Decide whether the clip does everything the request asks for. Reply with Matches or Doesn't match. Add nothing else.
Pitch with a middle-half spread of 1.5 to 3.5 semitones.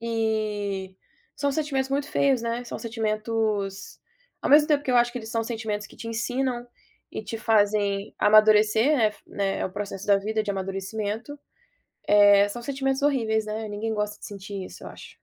Matches